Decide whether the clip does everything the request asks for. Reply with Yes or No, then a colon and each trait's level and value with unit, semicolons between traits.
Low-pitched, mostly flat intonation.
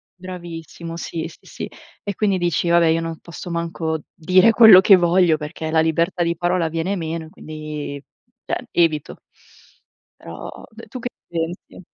No: medium, 170 Hz; narrow, 2.2 semitones